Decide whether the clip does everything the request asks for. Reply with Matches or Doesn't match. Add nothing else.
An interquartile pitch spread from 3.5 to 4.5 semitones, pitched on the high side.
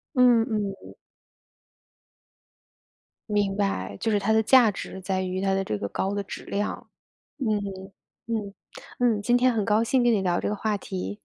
Doesn't match